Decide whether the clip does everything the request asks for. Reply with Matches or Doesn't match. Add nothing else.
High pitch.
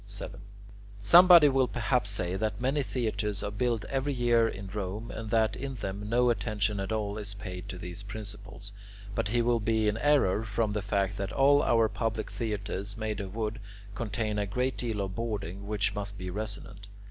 Doesn't match